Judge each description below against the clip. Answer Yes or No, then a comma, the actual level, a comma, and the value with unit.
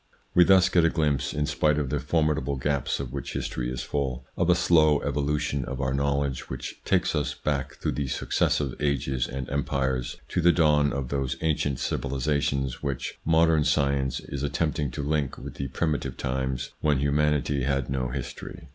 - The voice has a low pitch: Yes, very low, 70 Hz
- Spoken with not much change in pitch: Yes, narrow, 2.1 semitones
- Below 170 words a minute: No, average, 180 wpm